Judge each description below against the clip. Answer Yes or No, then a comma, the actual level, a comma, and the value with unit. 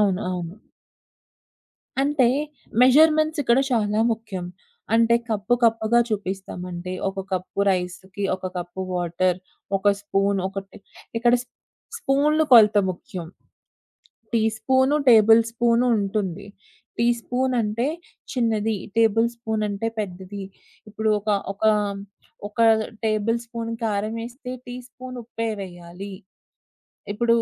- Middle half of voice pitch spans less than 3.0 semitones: No, average, 3.3 semitones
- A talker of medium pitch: No, high, 215 Hz